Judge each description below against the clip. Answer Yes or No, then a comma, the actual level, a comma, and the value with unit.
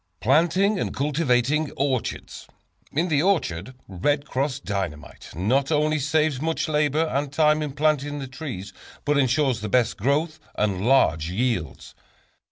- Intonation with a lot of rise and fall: No, average, 4.1 semitones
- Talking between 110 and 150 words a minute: Yes, average, 140 wpm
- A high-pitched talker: No, medium, 140 Hz